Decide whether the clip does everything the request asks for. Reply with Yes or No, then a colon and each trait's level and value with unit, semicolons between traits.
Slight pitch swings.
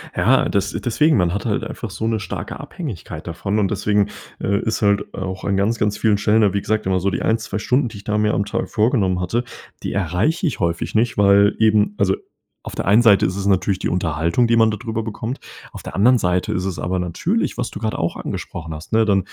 No: average, 3.1 semitones